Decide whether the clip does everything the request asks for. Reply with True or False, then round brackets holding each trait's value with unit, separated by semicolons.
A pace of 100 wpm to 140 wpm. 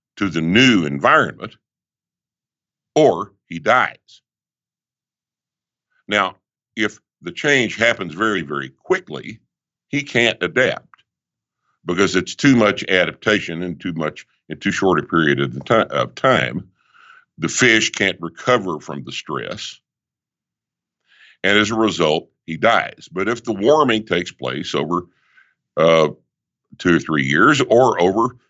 True (135 wpm)